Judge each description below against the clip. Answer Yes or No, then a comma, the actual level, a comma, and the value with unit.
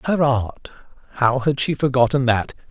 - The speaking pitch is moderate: No, low, 130 Hz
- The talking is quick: No, slow, 135 wpm